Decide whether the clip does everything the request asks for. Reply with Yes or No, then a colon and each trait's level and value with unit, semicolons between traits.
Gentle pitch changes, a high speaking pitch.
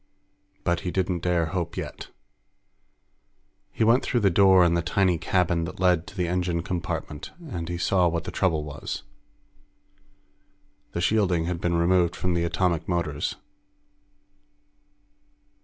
No: narrow, 1.6 semitones; very low, 85 Hz